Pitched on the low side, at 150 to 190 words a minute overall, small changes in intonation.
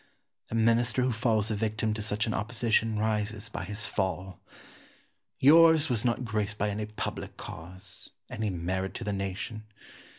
Yes: low, 110 Hz; average, 160 wpm; narrow, 2.1 semitones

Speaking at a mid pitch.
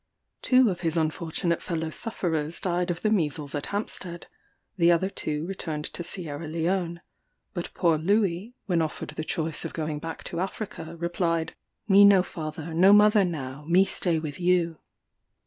Yes: medium, 170 Hz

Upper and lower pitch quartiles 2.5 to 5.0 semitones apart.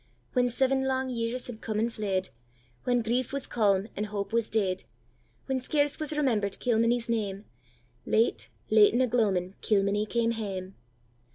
Yes: average, 4.0 semitones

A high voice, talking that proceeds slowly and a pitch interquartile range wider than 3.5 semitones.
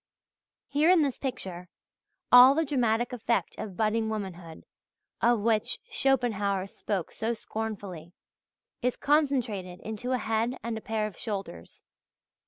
Yes: high, 220 Hz; slow, 130 wpm; average, 3.9 semitones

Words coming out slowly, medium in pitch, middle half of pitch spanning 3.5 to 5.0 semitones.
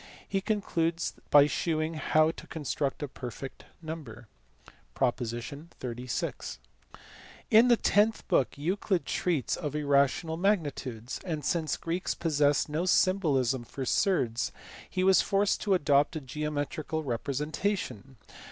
Yes: slow, 125 wpm; medium, 150 Hz; average, 4.5 semitones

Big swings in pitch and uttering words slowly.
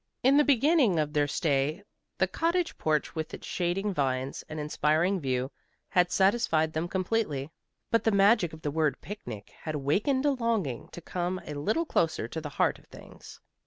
No: wide, 6.3 semitones; average, 180 wpm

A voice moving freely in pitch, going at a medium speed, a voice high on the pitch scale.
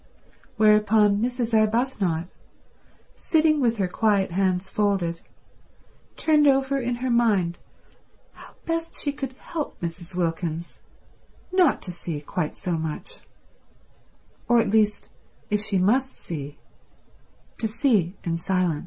No: wide, 6.0 semitones; slow, 120 wpm; high, 210 Hz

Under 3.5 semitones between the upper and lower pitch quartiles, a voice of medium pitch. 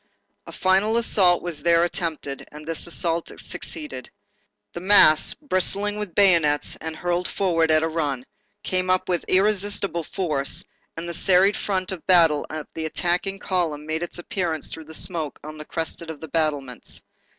Yes: average, 2.9 semitones; medium, 170 Hz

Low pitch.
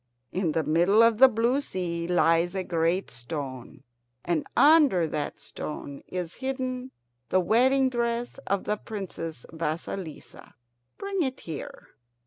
No: medium, 185 Hz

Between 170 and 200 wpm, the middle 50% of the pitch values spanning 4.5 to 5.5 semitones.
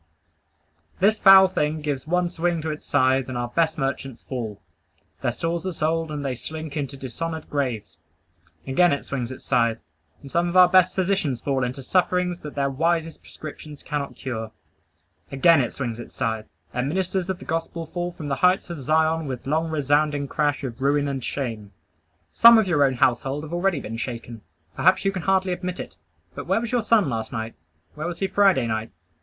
Yes: average, 195 wpm; average, 4.9 semitones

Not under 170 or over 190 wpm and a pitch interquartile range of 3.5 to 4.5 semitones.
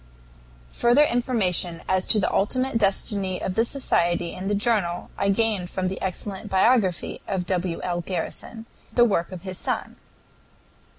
No: average, 155 wpm; average, 3.8 semitones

